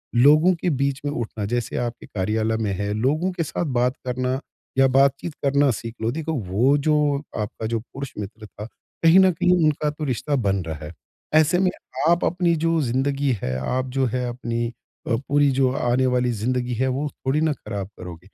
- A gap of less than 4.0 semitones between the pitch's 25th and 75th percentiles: No, average, 4.5 semitones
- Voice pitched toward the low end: Yes, low, 130 Hz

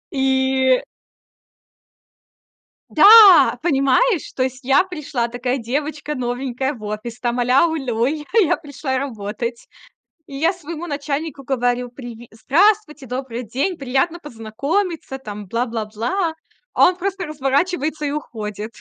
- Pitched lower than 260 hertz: No, very high, 270 Hz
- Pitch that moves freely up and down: No, average, 4.3 semitones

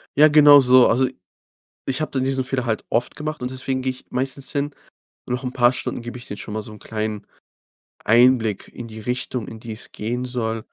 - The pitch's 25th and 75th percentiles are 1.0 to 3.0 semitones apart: Yes, average, 2.7 semitones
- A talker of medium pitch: No, low, 125 Hz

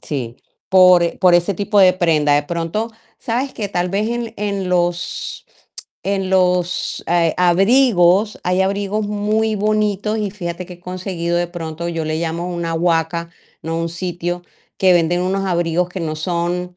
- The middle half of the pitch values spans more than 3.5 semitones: No, average, 2.7 semitones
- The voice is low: No, medium, 180 Hz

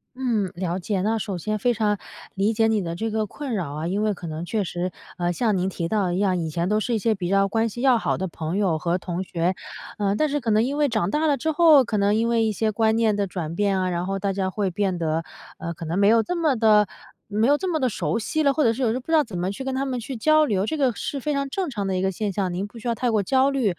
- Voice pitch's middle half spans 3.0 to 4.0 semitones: No, average, 4.6 semitones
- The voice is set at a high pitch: Yes, high, 210 Hz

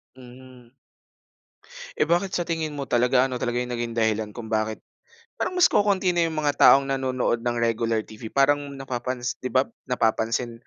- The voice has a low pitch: Yes, low, 125 Hz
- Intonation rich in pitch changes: No, average, 3.3 semitones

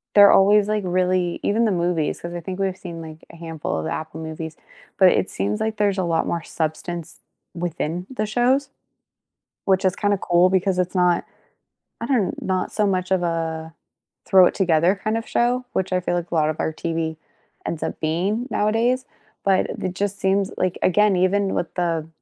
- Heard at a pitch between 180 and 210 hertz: Yes, medium, 185 Hz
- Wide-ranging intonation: No, average, 3.3 semitones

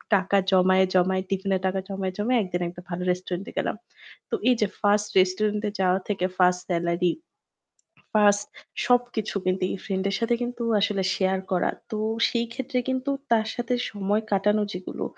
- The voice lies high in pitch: Yes, high, 195 Hz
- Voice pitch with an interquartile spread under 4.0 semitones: Yes, average, 2.7 semitones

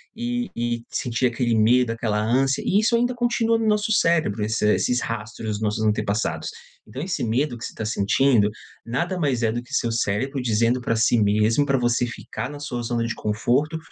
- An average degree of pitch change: Yes, average, 4.6 semitones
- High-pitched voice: No, low, 120 Hz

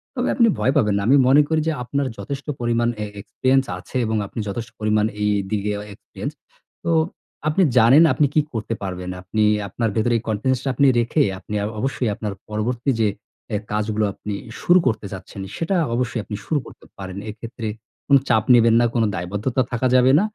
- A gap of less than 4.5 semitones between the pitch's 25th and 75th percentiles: Yes, average, 3.7 semitones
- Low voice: Yes, low, 115 Hz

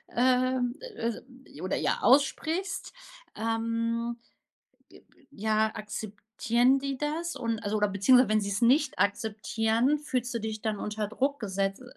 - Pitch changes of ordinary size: Yes, average, 3.2 semitones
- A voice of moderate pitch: No, high, 230 Hz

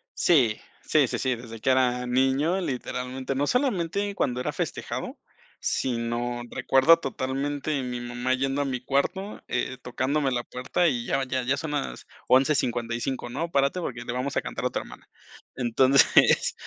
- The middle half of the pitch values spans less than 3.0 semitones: Yes, narrow, 2.6 semitones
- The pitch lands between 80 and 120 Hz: No, low, 130 Hz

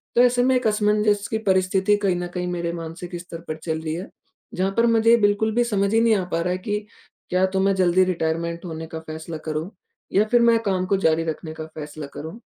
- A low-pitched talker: No, medium, 185 Hz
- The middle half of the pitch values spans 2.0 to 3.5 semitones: No, average, 4.1 semitones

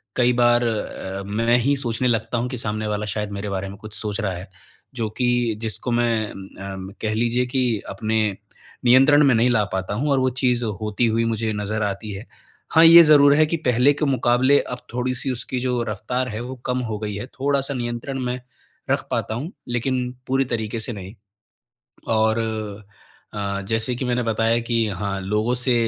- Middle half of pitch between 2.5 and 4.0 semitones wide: Yes, average, 2.9 semitones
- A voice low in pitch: Yes, low, 115 Hz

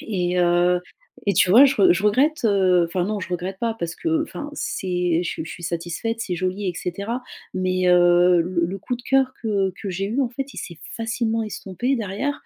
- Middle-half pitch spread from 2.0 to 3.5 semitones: No, average, 4.3 semitones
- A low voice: No, high, 190 Hz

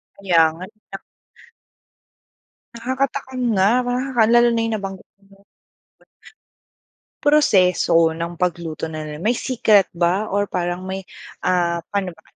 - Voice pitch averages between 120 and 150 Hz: No, high, 195 Hz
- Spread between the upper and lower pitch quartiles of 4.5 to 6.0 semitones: Yes, average, 5.1 semitones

